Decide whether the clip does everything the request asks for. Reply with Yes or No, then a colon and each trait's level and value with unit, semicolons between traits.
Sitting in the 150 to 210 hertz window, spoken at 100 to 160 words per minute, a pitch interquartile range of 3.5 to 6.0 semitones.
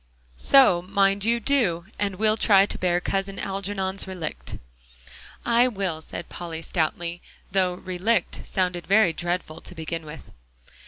No: high, 190 Hz; average, 140 wpm; narrow, 2.6 semitones